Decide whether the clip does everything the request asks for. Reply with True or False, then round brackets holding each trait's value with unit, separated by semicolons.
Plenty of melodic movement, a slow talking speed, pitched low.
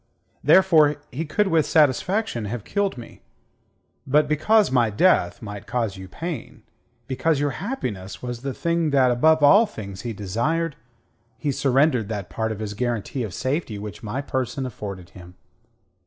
False (6.6 semitones; 155 wpm; 130 Hz)